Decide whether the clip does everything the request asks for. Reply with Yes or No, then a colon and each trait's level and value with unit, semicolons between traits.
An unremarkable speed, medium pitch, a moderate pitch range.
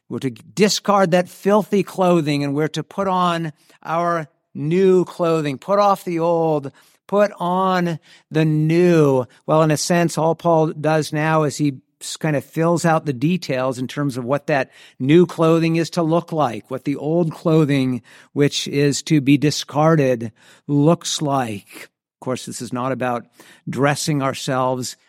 Yes: average, 165 wpm; medium, 155 Hz; average, 3.3 semitones